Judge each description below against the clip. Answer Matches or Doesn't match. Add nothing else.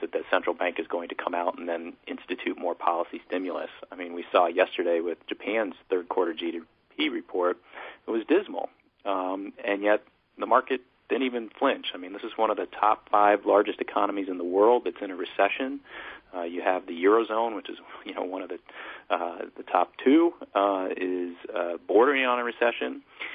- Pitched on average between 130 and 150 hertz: Doesn't match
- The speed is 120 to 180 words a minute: Doesn't match